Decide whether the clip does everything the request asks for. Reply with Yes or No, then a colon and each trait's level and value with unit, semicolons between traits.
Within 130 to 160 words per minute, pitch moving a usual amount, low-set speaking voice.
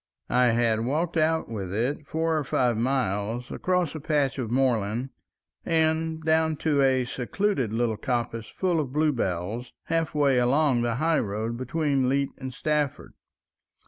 Yes: average, 150 wpm; average, 4.9 semitones; low, 130 Hz